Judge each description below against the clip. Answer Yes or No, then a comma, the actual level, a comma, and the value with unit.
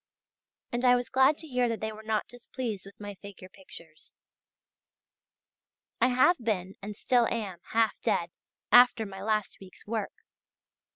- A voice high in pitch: Yes, high, 220 Hz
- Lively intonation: No, average, 3.7 semitones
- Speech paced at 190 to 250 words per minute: No, average, 155 wpm